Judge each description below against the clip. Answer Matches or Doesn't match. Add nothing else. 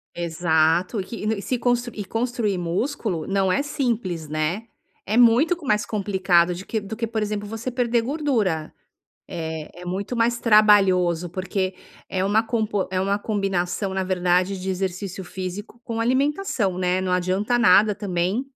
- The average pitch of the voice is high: Matches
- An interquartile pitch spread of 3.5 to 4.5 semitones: Matches